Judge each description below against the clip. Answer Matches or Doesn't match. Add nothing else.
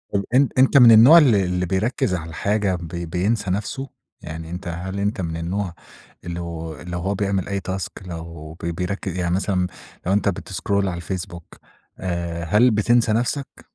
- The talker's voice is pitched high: Doesn't match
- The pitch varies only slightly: Doesn't match